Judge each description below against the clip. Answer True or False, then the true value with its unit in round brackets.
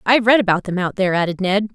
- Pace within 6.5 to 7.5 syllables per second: True (7.4 syllables/s)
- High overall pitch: True (200 Hz)